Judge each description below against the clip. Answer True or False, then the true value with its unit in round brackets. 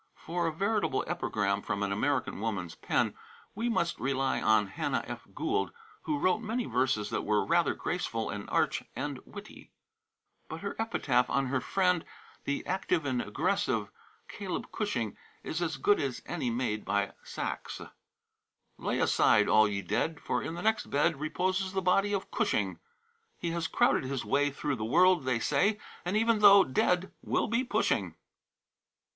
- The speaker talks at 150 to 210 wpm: True (165 wpm)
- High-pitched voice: False (160 Hz)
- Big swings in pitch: True (7.3 semitones)